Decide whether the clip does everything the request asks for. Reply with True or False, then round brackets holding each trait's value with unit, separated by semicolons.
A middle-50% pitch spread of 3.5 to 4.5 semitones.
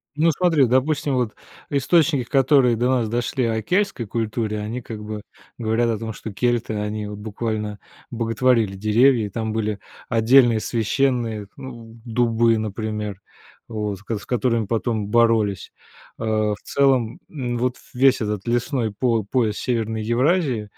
False (2.8 semitones)